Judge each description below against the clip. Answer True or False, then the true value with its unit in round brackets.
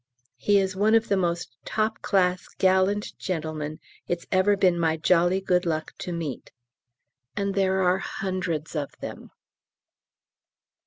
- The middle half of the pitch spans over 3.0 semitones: False (2.5 semitones)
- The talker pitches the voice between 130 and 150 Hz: False (185 Hz)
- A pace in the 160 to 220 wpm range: False (140 wpm)